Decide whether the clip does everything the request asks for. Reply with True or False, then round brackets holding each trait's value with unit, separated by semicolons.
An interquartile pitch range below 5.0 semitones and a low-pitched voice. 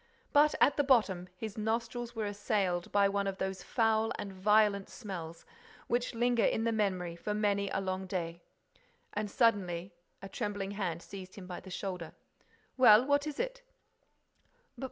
False (3.4 semitones; 205 Hz)